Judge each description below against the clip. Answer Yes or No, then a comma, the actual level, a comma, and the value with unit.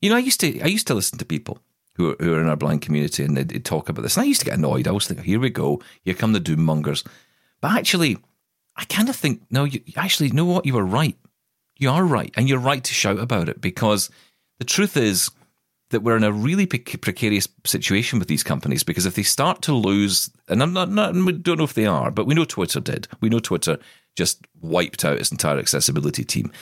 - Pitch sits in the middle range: No, low, 125 Hz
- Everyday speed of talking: No, fast, 250 wpm